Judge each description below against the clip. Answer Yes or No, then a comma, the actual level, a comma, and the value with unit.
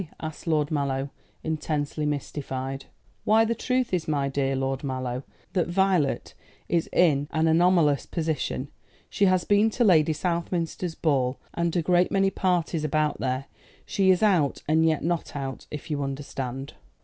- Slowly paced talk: No, average, 155 wpm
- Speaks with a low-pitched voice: No, medium, 155 Hz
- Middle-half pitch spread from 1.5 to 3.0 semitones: No, average, 4.3 semitones